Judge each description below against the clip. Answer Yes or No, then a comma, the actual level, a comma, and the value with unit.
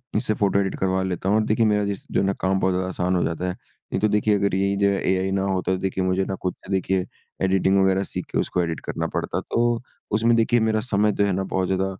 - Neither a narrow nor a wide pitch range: No, narrow, 1.5 semitones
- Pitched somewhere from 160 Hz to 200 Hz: No, very low, 95 Hz